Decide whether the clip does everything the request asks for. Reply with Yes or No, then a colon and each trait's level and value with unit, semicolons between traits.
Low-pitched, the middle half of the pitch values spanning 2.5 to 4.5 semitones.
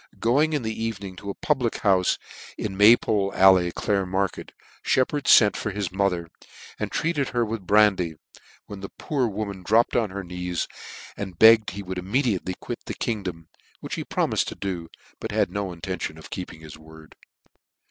Yes: low, 100 Hz; average, 3.5 semitones